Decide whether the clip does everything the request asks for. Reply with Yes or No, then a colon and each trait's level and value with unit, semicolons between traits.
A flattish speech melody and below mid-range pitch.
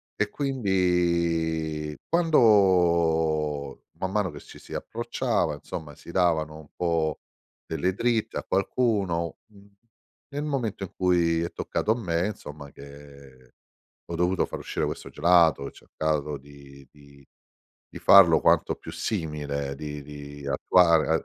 No: average, 4.4 semitones; very low, 85 Hz